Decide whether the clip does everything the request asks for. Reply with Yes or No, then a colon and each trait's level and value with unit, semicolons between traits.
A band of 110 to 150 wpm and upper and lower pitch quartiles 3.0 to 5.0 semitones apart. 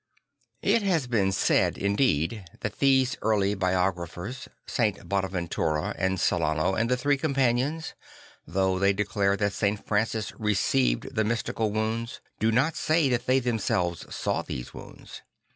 Yes: average, 140 wpm; average, 4.5 semitones